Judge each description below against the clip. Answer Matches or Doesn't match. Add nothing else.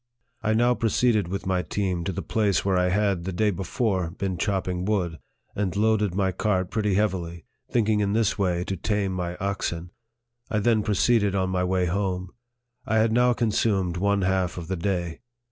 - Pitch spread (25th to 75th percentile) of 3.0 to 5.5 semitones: Doesn't match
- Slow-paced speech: Doesn't match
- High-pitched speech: Doesn't match